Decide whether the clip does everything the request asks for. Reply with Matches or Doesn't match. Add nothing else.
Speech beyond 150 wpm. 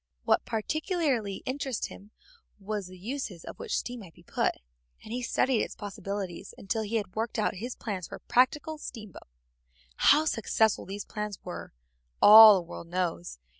Matches